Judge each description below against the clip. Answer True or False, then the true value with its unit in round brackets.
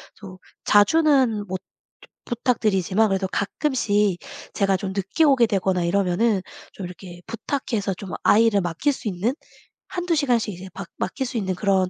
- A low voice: False (205 Hz)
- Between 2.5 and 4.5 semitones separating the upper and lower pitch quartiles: True (3.8 semitones)